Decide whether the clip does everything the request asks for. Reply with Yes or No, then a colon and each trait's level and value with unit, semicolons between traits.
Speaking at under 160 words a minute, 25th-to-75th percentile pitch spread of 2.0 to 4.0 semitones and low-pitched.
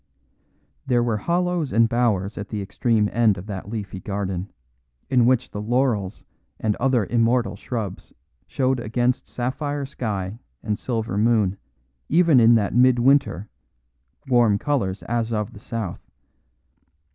Yes: slow, 135 wpm; average, 3.5 semitones; low, 115 Hz